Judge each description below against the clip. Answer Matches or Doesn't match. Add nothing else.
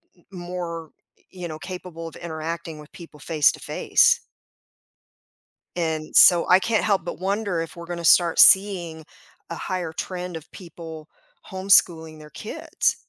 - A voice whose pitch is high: Doesn't match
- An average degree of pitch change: Doesn't match